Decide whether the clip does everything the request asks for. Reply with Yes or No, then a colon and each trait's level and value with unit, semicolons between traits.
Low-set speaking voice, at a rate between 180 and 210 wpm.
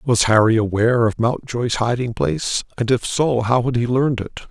Yes: low, 120 Hz; average, 200 wpm